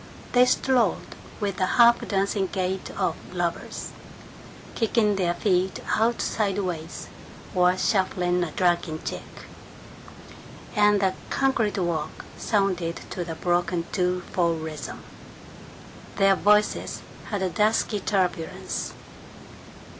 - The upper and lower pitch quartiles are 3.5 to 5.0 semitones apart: No, average, 2.8 semitones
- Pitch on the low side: No, high, 190 Hz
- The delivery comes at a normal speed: No, slow, 110 wpm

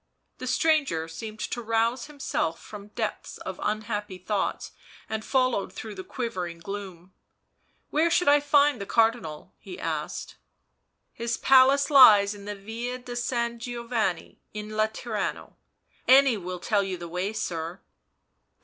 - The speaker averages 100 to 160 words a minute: Yes, average, 150 wpm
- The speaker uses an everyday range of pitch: Yes, average, 4.0 semitones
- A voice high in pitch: Yes, high, 220 Hz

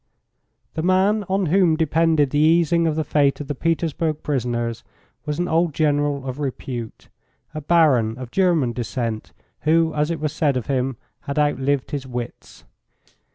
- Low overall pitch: No, medium, 150 Hz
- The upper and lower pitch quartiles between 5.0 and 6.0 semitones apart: No, average, 3.8 semitones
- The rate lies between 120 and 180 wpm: Yes, average, 160 wpm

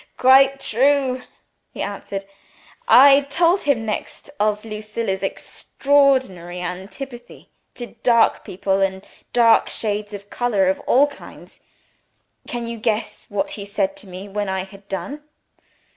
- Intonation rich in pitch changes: No, average, 5.0 semitones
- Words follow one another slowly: Yes, slow, 130 wpm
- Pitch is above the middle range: Yes, high, 215 Hz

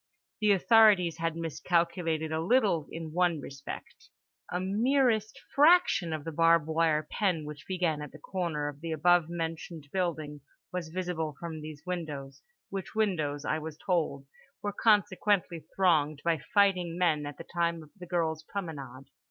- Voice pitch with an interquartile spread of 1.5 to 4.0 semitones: Yes, average, 2.9 semitones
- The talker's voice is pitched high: No, medium, 165 Hz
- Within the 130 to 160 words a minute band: Yes, average, 155 wpm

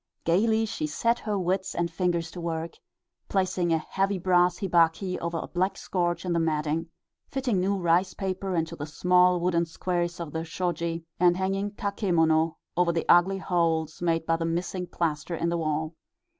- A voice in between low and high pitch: Yes, medium, 175 Hz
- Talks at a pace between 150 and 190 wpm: Yes, average, 175 wpm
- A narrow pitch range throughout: Yes, narrow, 2.2 semitones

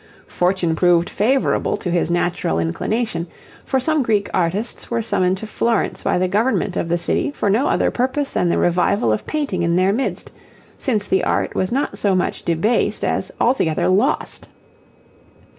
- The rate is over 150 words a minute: Yes, average, 170 wpm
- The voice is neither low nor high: No, high, 195 Hz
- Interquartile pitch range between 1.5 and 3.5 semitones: No, average, 5.2 semitones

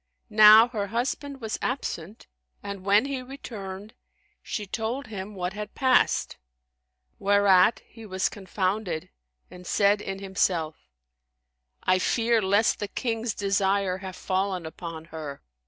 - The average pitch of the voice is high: Yes, high, 200 Hz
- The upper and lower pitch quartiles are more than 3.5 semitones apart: No, average, 2.9 semitones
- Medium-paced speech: No, slow, 125 wpm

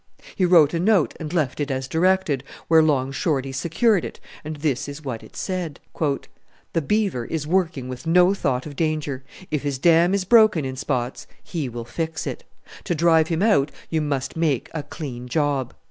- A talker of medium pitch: Yes, medium, 155 Hz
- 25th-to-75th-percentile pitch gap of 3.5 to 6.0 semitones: Yes, average, 4.0 semitones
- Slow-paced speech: No, average, 190 wpm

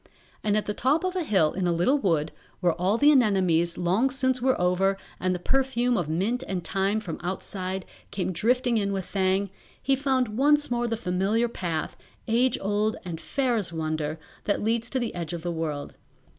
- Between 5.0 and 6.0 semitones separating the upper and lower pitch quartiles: Yes, wide, 5.6 semitones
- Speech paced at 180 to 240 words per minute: Yes, average, 200 wpm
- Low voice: No, high, 200 Hz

